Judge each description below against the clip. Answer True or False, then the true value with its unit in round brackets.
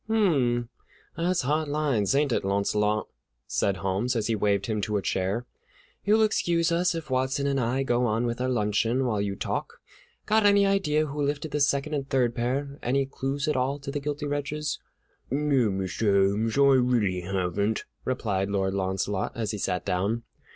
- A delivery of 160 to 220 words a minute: True (180 wpm)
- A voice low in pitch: True (125 Hz)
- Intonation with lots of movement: True (5.8 semitones)